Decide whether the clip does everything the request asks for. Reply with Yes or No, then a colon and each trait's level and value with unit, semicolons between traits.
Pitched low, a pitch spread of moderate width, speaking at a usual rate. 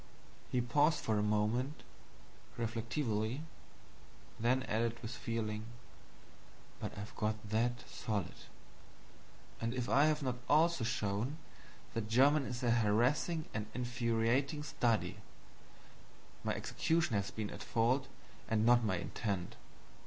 No: low, 115 Hz; average, 3.3 semitones; slow, 120 wpm